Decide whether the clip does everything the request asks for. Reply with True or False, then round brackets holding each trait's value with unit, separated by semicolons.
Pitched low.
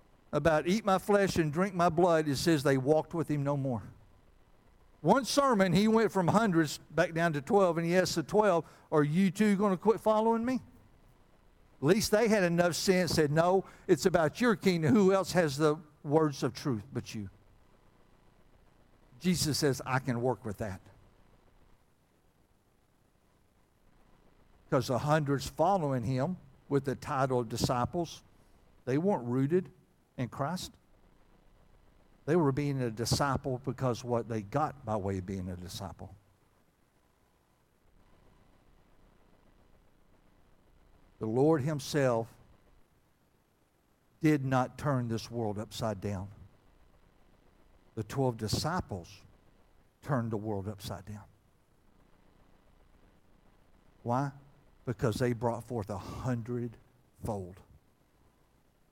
True (130 Hz)